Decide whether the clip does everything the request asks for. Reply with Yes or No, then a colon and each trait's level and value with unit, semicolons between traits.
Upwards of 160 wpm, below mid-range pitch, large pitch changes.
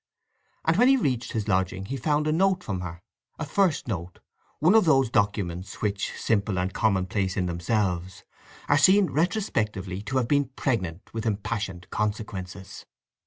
No: average, 150 wpm; low, 105 Hz; wide, 7.4 semitones